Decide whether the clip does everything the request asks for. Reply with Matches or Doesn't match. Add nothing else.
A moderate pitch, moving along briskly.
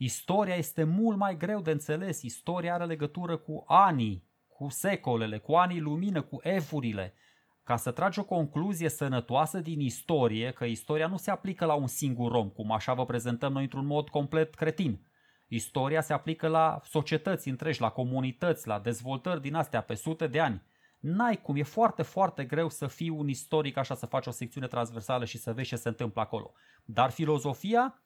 Matches